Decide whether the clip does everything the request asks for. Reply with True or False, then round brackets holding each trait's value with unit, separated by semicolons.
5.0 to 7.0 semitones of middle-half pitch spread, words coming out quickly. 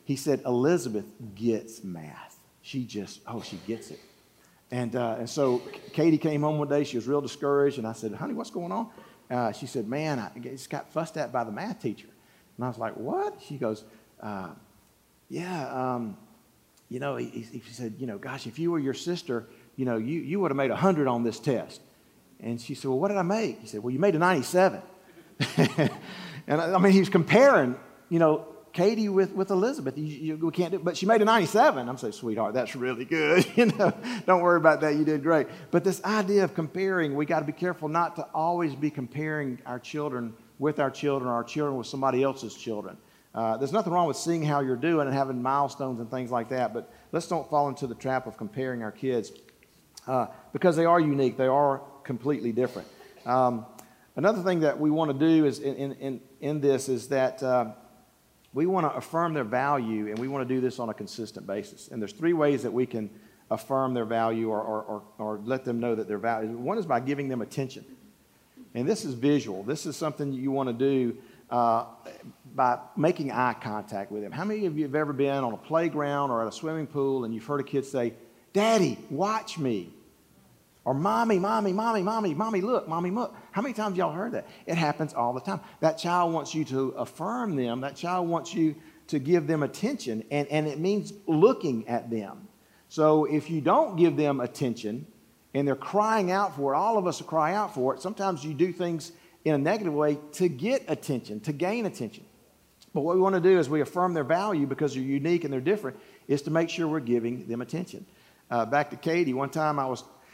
True (5.3 semitones; 220 wpm)